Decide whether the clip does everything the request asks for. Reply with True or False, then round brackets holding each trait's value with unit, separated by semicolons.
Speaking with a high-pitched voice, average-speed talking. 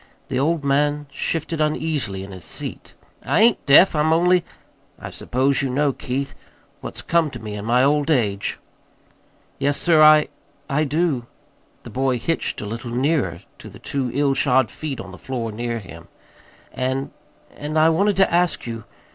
False (140 Hz; 170 wpm)